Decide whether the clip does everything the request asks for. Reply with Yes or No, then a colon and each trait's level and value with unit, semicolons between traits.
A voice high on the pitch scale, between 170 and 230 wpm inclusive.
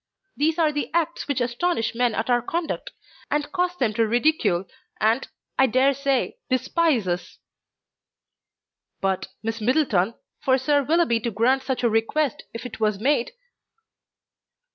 No: very high, 255 Hz; average, 145 wpm